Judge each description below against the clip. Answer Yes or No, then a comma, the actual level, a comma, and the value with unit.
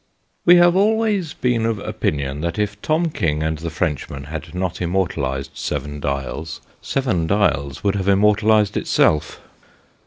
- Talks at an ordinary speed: Yes, average, 155 wpm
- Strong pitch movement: Yes, wide, 6.9 semitones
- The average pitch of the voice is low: Yes, very low, 90 Hz